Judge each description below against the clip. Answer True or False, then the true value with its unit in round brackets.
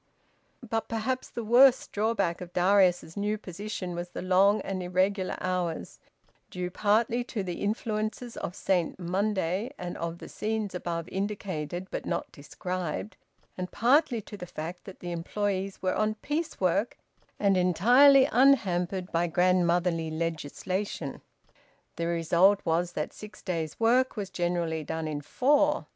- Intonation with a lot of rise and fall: False (3.6 semitones)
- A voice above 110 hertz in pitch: True (185 Hz)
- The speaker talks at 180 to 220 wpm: False (145 wpm)